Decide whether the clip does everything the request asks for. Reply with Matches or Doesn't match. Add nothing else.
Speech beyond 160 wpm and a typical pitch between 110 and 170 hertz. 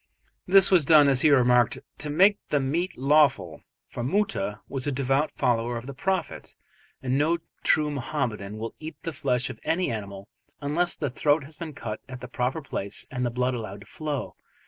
Matches